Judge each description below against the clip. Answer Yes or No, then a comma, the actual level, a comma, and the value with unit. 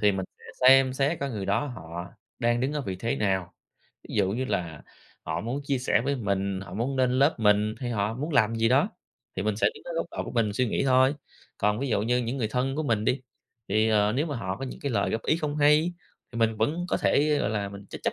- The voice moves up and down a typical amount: Yes, average, 4.7 semitones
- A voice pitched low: Yes, low, 115 Hz